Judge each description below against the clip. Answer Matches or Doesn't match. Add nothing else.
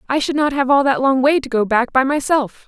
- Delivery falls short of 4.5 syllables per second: Doesn't match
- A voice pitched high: Matches